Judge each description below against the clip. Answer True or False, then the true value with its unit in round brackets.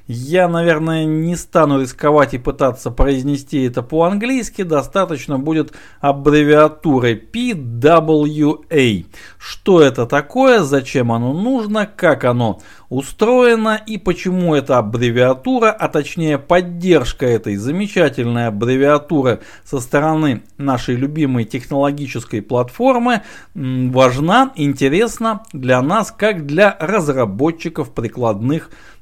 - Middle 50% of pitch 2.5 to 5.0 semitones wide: False (5.4 semitones)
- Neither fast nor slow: False (95 wpm)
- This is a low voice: False (150 Hz)